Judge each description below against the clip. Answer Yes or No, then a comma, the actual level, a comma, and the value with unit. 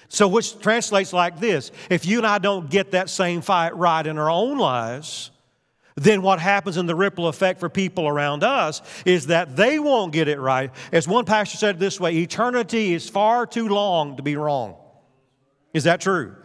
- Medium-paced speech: Yes, average, 195 wpm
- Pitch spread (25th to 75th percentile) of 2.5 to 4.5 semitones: No, average, 5.3 semitones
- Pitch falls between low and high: Yes, medium, 180 Hz